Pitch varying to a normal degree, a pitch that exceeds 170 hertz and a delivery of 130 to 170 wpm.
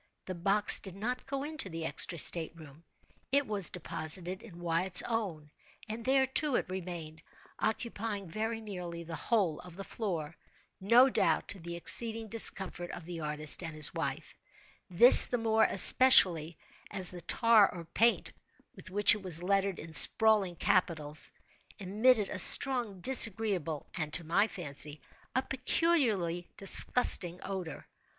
Yes: average, 4.9 semitones; high, 190 Hz; average, 145 wpm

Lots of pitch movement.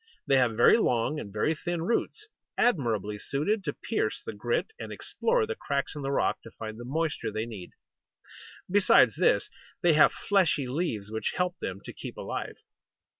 Yes: wide, 8.2 semitones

